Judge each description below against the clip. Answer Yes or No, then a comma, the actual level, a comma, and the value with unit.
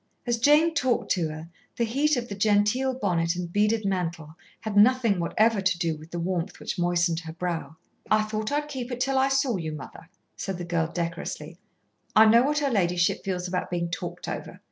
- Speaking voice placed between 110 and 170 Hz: No, high, 195 Hz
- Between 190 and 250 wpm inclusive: Yes, fast, 205 wpm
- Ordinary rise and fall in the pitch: No, wide, 5.8 semitones